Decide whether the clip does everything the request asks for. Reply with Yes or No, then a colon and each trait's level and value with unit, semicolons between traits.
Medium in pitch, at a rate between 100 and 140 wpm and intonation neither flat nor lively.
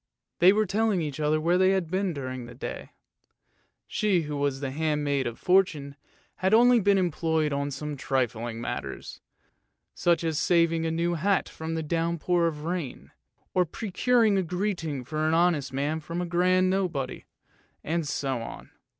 No: medium, 165 Hz; average, 165 wpm; average, 4.1 semitones